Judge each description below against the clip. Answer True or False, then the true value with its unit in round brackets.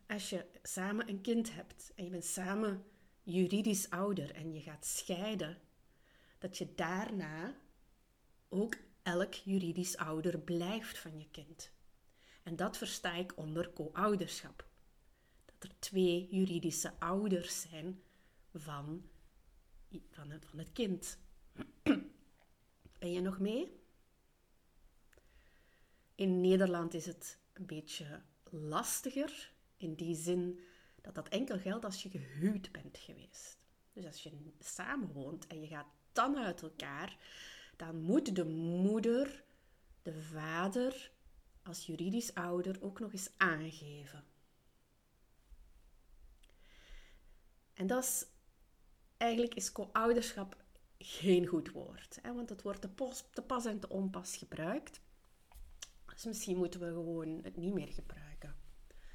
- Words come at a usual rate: False (120 wpm)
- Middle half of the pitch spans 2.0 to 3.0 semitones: False (3.9 semitones)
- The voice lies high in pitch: False (180 Hz)